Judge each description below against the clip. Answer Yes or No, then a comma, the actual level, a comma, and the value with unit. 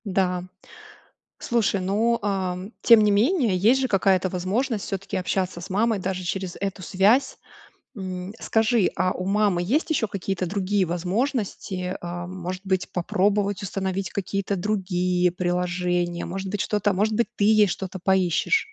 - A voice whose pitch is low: No, high, 190 Hz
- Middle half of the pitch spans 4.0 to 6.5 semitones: No, narrow, 2.4 semitones